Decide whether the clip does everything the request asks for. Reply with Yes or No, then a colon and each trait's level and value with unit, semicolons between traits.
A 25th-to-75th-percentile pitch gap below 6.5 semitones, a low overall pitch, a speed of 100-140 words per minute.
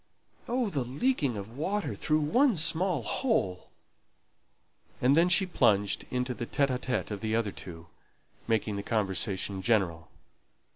No: wide, 8.4 semitones; low, 125 Hz; slow, 135 wpm